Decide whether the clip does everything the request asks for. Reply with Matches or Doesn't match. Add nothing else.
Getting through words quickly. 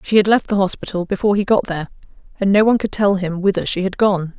Matches